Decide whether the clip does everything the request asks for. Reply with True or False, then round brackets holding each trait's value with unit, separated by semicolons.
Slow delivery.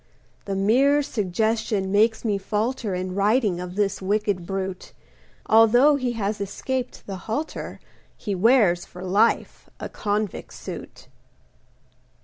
True (125 wpm)